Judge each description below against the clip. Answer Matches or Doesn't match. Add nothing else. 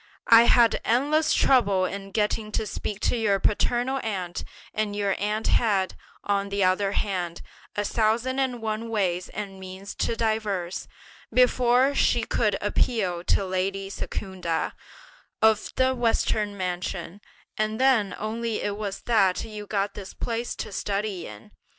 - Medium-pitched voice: Doesn't match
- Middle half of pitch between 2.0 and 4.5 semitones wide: Matches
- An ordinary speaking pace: Matches